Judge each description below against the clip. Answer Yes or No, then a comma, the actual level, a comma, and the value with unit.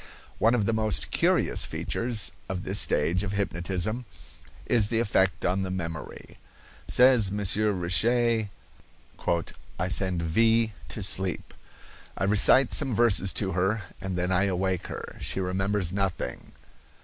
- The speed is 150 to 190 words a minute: No, slow, 135 wpm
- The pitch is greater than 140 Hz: No, low, 100 Hz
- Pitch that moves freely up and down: No, average, 3.1 semitones